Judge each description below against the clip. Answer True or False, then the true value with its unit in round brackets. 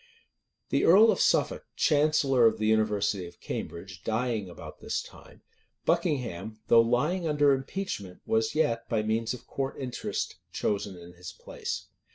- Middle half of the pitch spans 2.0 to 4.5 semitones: False (5.2 semitones)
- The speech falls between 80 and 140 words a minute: False (150 wpm)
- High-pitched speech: False (115 Hz)